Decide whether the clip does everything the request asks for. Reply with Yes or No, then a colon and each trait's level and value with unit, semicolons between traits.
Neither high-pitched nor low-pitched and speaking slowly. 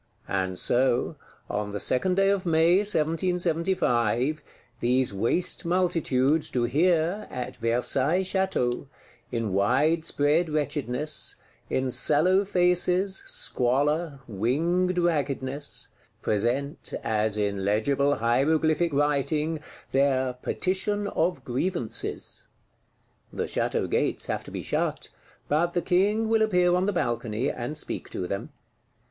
Yes: medium, 150 Hz; slow, 115 wpm